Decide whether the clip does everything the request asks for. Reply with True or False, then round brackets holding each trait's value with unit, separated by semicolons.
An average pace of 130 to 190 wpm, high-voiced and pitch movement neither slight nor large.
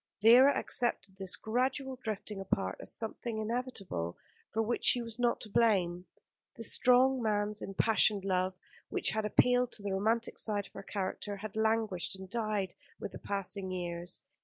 True (160 wpm; 215 Hz; 3.3 semitones)